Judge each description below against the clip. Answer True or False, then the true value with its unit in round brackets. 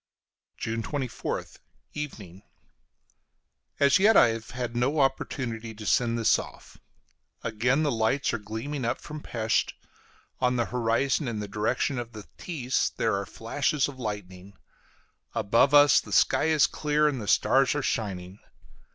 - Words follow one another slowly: False (150 wpm)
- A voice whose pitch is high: False (120 Hz)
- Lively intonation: False (4.2 semitones)